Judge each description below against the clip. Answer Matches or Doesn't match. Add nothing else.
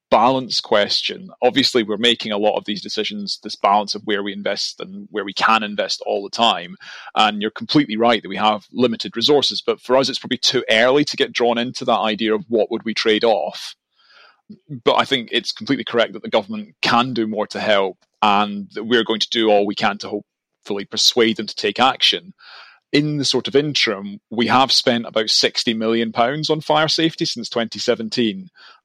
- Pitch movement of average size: Matches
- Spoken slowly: Doesn't match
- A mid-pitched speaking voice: Doesn't match